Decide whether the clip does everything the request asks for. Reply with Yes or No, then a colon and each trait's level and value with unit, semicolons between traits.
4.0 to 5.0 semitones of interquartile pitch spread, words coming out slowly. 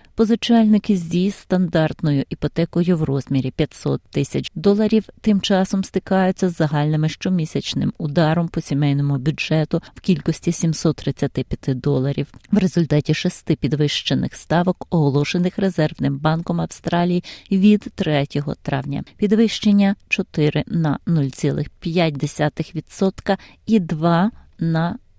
Yes: average, 4.3 semitones; slow, 100 wpm